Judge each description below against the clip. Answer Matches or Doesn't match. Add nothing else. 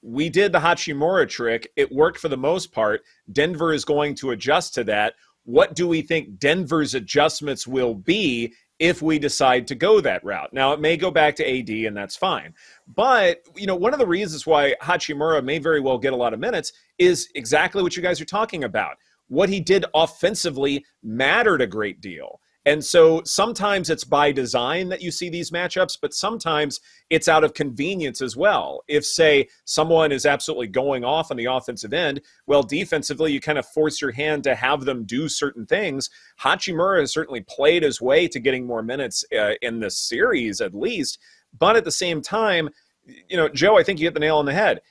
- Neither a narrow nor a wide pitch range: Matches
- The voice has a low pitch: Doesn't match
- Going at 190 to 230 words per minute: Matches